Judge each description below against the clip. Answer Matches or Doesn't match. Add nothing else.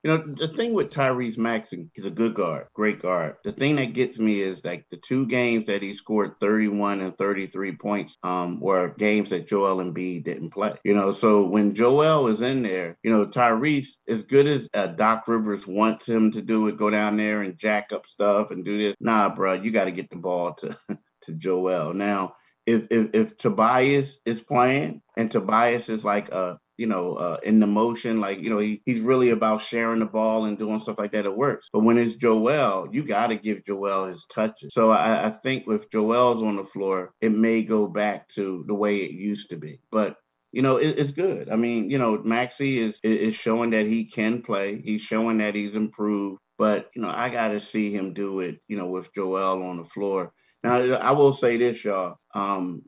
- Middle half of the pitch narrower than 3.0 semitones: Matches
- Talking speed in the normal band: Doesn't match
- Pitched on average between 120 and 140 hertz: Doesn't match